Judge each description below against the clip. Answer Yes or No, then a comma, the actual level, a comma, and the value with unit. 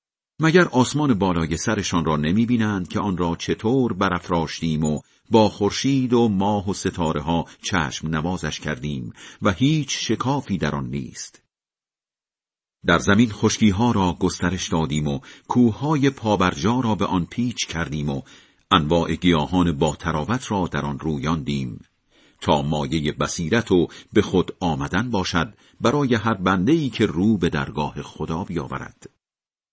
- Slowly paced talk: No, average, 140 wpm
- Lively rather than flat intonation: Yes, wide, 6.0 semitones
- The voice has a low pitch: Yes, very low, 95 Hz